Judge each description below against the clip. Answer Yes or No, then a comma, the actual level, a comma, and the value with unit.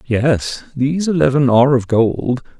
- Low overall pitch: Yes, low, 130 Hz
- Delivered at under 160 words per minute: Yes, average, 140 wpm